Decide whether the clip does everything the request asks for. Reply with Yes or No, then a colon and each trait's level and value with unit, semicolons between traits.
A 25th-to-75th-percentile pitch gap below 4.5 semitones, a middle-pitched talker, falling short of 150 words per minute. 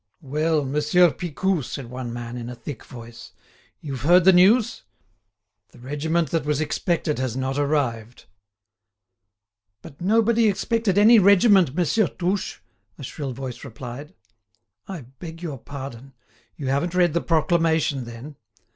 No: average, 5.3 semitones; medium, 150 Hz; average, 140 wpm